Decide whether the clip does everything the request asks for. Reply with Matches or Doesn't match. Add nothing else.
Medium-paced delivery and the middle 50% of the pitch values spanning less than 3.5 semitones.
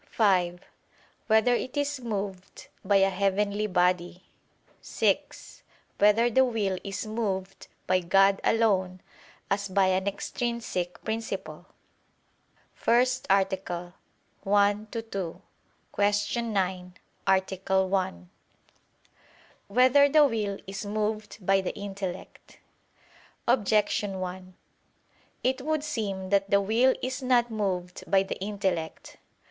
Doesn't match